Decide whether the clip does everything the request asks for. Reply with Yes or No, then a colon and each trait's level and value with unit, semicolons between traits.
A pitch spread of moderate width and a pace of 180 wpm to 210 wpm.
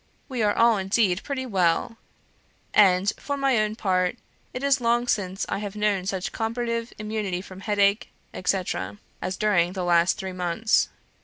No: average, 3.7 semitones; average, 160 wpm